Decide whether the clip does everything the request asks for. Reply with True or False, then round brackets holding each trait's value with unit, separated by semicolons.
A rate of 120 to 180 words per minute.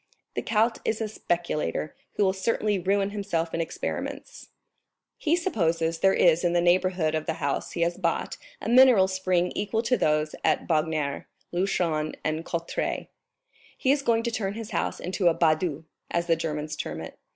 True (175 wpm)